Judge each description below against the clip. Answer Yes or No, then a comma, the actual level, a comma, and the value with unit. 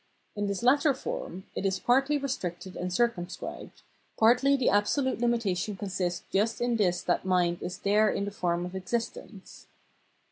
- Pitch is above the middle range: Yes, high, 205 Hz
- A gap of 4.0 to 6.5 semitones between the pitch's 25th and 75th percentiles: Yes, average, 4.8 semitones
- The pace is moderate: Yes, average, 165 wpm